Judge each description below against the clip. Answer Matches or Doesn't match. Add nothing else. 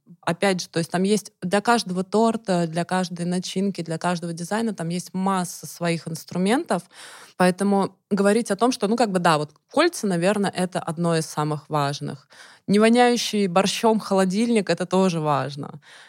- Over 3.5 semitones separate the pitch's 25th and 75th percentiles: Doesn't match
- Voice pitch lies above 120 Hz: Matches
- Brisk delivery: Matches